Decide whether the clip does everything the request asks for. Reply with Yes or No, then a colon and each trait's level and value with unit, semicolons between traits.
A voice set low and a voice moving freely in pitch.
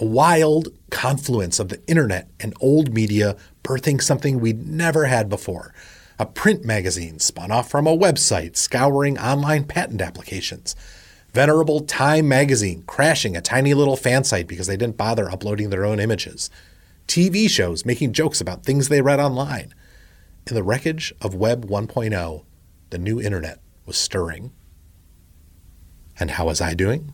Yes: low, 110 Hz; wide, 7.8 semitones